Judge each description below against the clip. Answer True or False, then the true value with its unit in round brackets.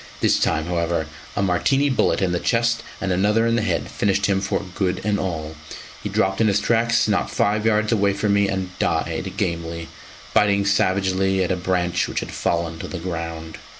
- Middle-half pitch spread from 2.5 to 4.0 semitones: True (2.9 semitones)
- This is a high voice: False (95 Hz)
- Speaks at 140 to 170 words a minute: False (195 wpm)